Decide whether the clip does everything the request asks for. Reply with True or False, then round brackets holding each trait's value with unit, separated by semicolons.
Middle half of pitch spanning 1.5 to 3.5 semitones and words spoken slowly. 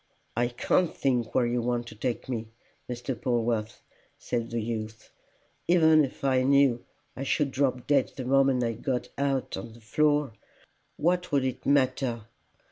False (2.8 semitones; 160 wpm)